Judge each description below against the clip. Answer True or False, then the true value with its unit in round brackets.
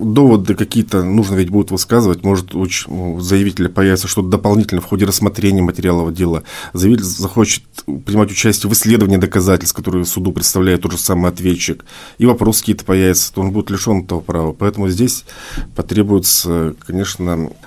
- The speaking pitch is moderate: False (95 Hz)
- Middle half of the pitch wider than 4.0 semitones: False (2.7 semitones)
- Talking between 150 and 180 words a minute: True (155 wpm)